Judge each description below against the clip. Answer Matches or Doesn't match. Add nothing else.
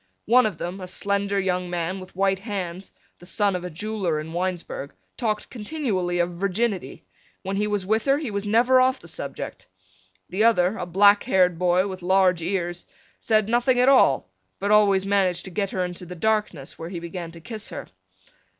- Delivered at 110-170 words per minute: Doesn't match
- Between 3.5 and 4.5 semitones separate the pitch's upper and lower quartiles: Doesn't match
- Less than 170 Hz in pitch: Doesn't match